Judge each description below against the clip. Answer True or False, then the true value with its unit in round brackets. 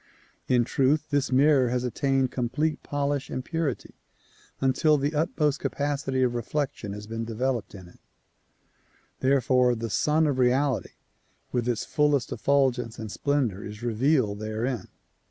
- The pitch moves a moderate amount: True (3.4 semitones)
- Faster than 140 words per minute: False (135 wpm)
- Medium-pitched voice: False (130 Hz)